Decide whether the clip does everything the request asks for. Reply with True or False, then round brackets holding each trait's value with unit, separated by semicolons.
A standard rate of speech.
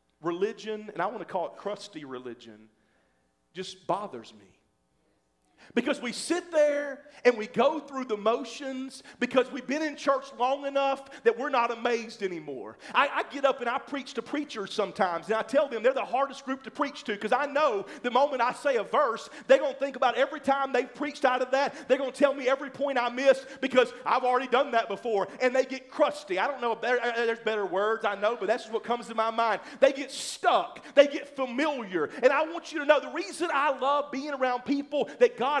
False (220 wpm)